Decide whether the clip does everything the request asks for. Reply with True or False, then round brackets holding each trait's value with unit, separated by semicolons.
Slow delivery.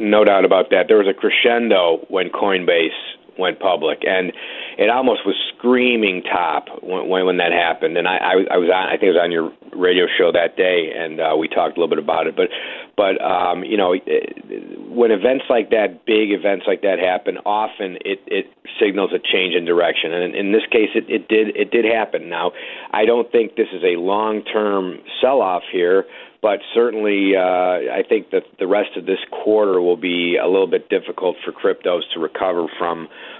False (205 wpm)